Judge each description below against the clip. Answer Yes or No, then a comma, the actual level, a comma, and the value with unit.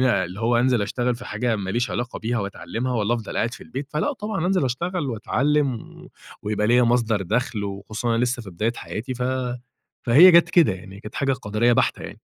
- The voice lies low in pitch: Yes, low, 120 Hz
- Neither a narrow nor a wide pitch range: Yes, average, 3.3 semitones